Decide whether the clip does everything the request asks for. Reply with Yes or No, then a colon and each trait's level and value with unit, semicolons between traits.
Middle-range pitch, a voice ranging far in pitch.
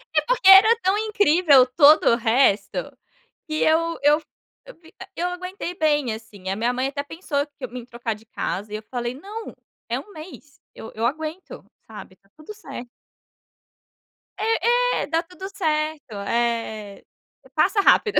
No: very high, 300 Hz; wide, 7.4 semitones